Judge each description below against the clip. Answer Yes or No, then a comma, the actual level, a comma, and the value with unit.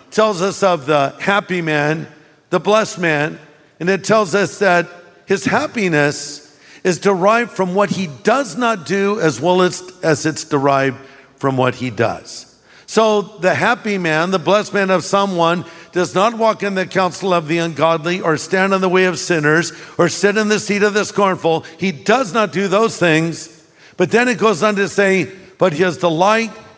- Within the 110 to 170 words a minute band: No, average, 190 wpm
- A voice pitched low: No, medium, 185 Hz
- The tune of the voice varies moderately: Yes, average, 4.0 semitones